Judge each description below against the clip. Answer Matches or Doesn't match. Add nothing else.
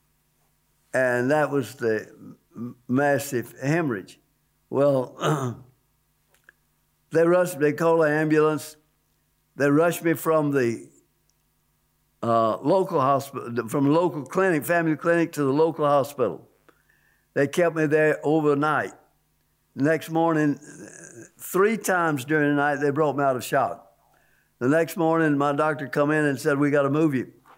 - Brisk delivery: Doesn't match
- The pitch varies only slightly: Doesn't match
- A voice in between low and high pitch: Matches